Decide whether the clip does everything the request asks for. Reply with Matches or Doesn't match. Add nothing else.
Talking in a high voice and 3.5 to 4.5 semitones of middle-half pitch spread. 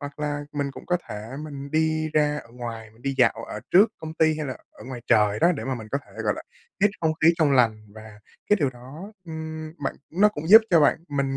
Doesn't match